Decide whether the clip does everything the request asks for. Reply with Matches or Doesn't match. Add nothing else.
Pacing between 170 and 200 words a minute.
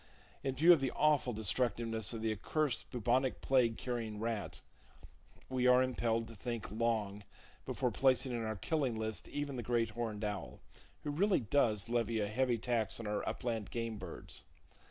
Matches